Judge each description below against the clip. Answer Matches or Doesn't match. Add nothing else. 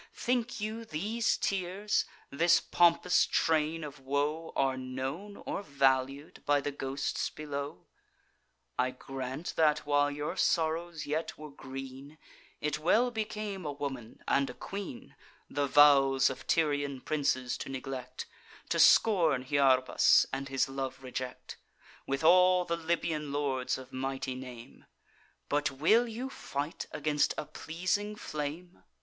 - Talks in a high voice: Doesn't match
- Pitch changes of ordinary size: Matches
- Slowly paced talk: Matches